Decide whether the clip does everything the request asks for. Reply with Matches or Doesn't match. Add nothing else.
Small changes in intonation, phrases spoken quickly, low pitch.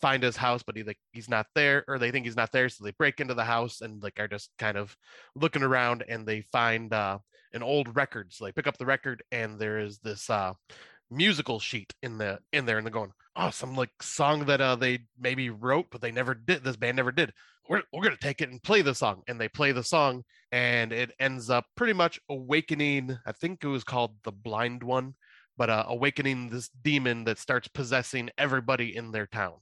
Doesn't match